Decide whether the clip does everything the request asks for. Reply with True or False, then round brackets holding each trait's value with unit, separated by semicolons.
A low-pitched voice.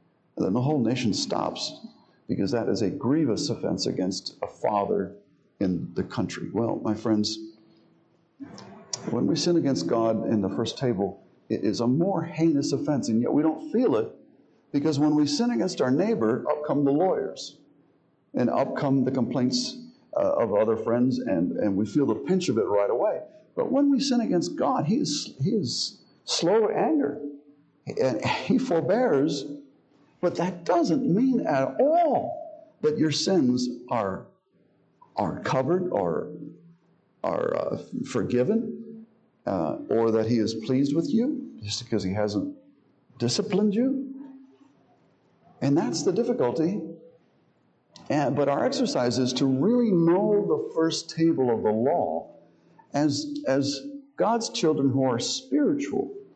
False (155 Hz)